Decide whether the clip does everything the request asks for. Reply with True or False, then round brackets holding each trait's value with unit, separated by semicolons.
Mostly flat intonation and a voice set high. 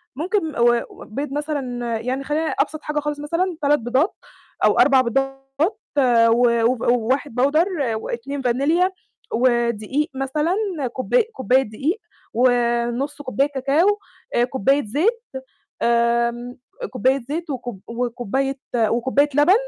False (3.7 semitones; 265 Hz)